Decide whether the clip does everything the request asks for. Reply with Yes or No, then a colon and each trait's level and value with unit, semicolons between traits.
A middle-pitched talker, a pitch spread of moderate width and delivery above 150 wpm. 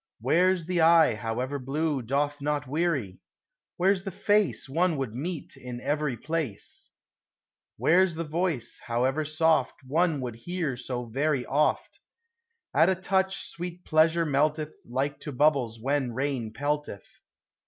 No: medium, 150 Hz; average, 4.3 semitones; average, 145 wpm